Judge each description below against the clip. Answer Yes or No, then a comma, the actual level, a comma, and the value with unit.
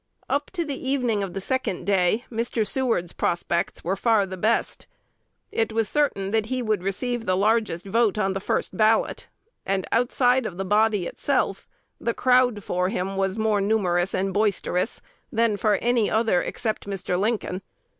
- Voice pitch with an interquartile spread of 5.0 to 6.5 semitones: No, average, 3.3 semitones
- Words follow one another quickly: No, average, 170 wpm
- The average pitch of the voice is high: Yes, high, 215 Hz